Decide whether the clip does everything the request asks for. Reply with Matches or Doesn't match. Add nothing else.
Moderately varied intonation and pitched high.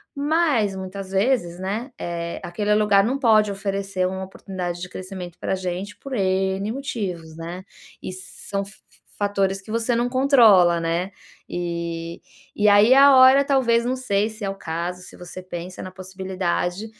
Matches